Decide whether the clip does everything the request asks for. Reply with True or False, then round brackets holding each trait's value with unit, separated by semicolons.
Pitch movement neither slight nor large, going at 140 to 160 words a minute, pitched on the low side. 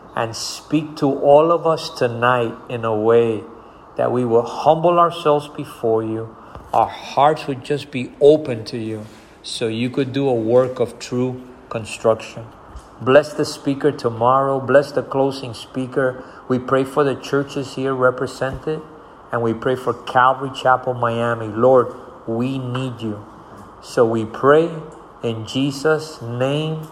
True (3.5 semitones; 145 wpm; 130 Hz)